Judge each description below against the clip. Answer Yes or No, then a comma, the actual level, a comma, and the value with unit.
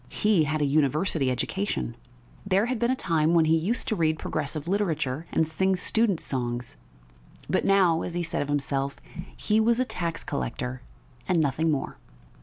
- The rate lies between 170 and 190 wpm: Yes, average, 180 wpm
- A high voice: No, medium, 160 Hz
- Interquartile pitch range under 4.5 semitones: No, average, 5.1 semitones